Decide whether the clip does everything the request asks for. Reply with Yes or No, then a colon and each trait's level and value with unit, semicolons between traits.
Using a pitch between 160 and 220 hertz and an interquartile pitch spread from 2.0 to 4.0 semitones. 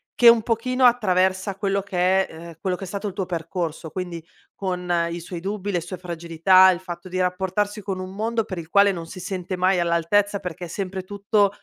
Yes: medium, 185 Hz; narrow, 2.4 semitones